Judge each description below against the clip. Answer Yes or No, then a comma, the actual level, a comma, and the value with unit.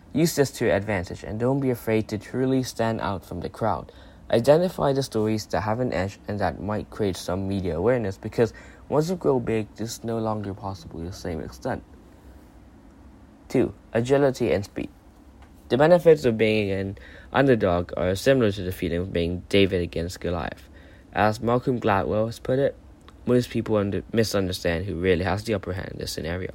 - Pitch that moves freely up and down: No, average, 4.2 semitones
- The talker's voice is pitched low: Yes, low, 105 Hz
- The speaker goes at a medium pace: Yes, average, 190 wpm